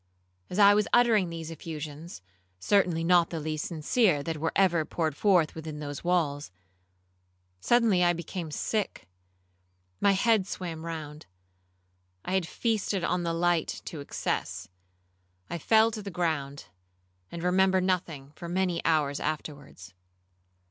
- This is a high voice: No, medium, 165 Hz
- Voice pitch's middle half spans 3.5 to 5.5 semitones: Yes, average, 4.2 semitones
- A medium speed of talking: No, slow, 130 wpm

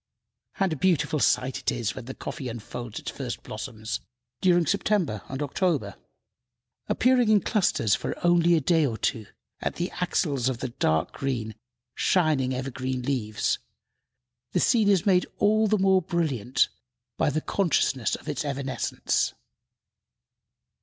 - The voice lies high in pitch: No, medium, 145 Hz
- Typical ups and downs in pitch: No, wide, 6.5 semitones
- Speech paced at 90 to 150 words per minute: Yes, average, 145 wpm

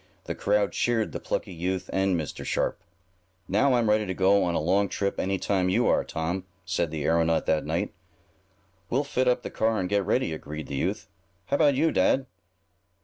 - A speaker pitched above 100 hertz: No, very low, 95 Hz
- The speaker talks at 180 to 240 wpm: Yes, average, 200 wpm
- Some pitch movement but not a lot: Yes, average, 4.4 semitones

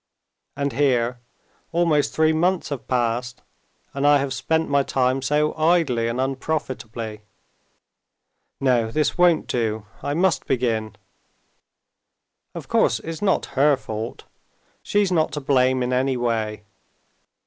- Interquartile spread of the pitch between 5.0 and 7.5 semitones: No, average, 4.3 semitones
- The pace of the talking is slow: Yes, slow, 125 wpm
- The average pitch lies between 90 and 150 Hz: Yes, low, 135 Hz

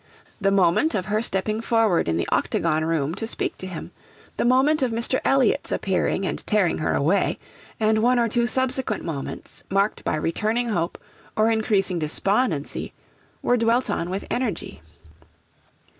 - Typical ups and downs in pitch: Yes, average, 5.0 semitones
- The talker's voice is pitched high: Yes, high, 210 Hz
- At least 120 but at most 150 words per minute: No, average, 160 wpm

